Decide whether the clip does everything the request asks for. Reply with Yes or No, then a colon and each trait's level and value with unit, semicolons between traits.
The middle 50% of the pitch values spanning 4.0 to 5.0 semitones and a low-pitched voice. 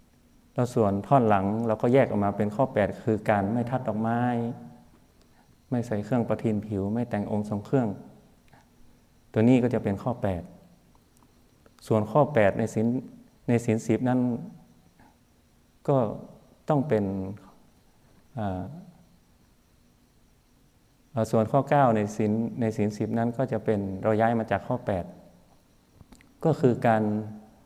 No: average, 2.7 semitones; low, 110 Hz